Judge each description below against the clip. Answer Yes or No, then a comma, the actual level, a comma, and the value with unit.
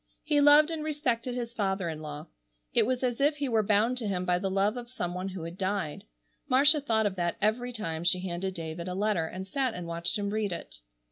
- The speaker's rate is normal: No, fast, 240 wpm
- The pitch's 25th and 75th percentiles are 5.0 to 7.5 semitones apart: Yes, wide, 5.6 semitones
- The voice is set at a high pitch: Yes, high, 205 Hz